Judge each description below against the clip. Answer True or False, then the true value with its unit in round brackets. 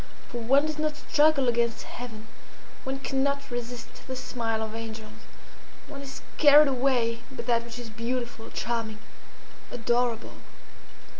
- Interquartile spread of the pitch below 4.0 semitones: True (2.7 semitones)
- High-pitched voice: True (245 Hz)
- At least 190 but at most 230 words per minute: False (135 wpm)